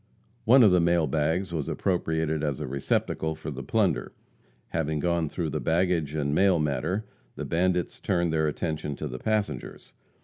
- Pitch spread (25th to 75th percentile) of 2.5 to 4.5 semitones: Yes, average, 2.9 semitones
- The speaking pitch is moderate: No, very low, 80 Hz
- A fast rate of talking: No, average, 170 wpm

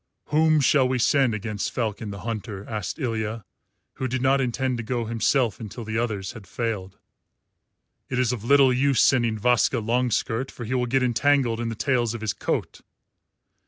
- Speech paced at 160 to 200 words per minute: Yes, average, 180 wpm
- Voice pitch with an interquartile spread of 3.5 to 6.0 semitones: No, average, 2.8 semitones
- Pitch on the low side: Yes, low, 120 Hz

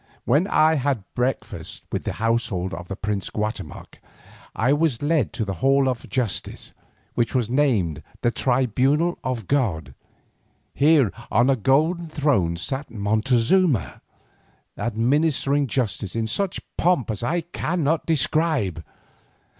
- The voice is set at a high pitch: No, low, 130 Hz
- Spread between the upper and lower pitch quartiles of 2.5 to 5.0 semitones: No, wide, 5.4 semitones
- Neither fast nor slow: No, slow, 130 wpm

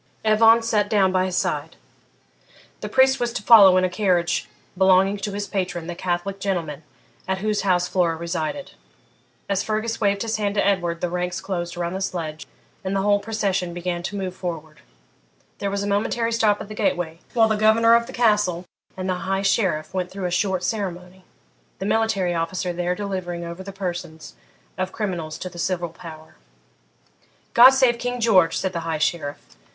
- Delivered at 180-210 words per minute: Yes, average, 190 wpm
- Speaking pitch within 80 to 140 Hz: No, high, 190 Hz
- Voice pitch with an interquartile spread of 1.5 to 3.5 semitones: Yes, average, 3.0 semitones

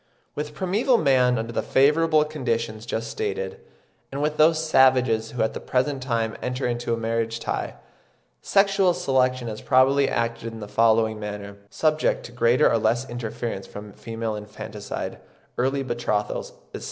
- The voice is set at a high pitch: No, low, 120 Hz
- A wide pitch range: No, average, 4.0 semitones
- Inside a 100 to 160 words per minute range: Yes, average, 155 wpm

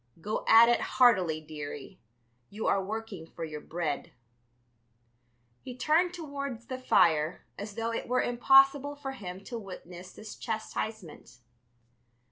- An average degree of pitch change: No, wide, 6.4 semitones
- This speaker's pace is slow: Yes, slow, 130 wpm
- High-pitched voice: Yes, high, 220 Hz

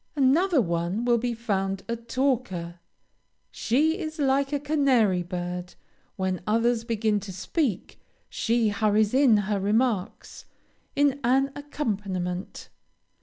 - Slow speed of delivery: Yes, slow, 120 wpm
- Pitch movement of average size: No, wide, 5.7 semitones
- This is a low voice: No, high, 230 Hz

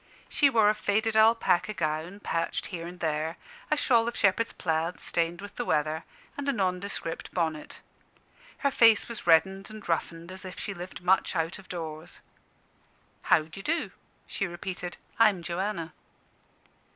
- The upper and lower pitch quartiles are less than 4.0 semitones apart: No, average, 4.3 semitones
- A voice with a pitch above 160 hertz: Yes, medium, 185 Hz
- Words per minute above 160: No, average, 155 wpm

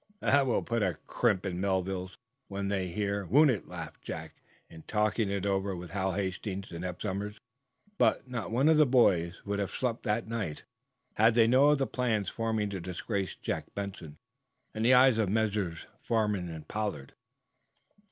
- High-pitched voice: No, low, 100 Hz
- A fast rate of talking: No, average, 180 wpm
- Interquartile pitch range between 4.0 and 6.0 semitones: No, average, 3.4 semitones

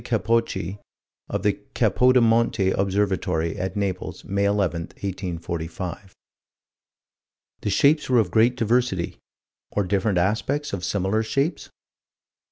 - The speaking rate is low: Yes, slow, 105 wpm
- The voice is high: No, low, 100 Hz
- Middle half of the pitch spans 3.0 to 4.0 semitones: Yes, average, 3.7 semitones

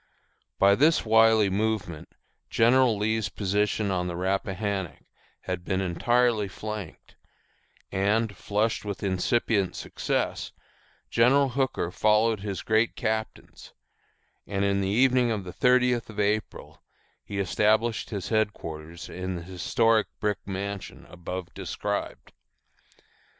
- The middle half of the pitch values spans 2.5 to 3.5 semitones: Yes, average, 2.8 semitones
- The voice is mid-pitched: No, low, 105 Hz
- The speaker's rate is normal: No, slow, 115 wpm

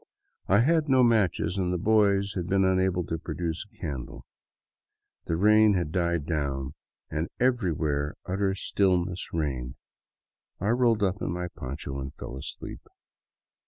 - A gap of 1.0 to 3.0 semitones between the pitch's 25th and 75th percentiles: No, average, 4.5 semitones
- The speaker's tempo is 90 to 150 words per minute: Yes, average, 145 wpm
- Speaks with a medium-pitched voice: No, very low, 90 Hz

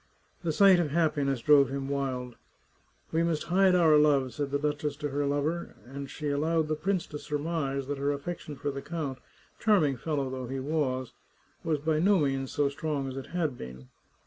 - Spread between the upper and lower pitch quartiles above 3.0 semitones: No, narrow, 2.6 semitones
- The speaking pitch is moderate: Yes, medium, 145 Hz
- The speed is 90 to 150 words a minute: No, average, 195 wpm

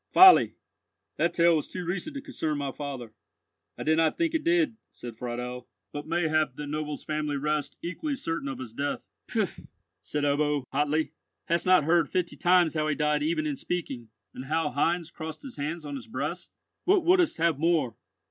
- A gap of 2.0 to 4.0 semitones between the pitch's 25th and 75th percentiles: Yes, average, 3.3 semitones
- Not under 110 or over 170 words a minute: No, average, 185 wpm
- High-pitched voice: No, medium, 155 Hz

